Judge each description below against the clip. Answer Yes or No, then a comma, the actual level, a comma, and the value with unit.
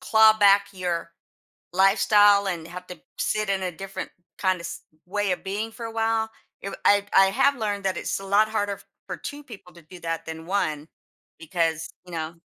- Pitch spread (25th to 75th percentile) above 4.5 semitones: No, average, 3.0 semitones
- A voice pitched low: No, high, 195 Hz